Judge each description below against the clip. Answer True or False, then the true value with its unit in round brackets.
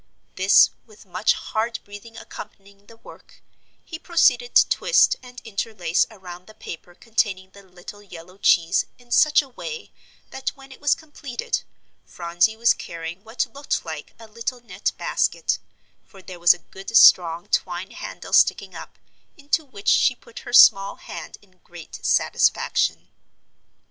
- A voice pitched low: False (205 Hz)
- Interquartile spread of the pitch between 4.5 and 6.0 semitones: True (5.0 semitones)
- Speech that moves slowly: False (155 wpm)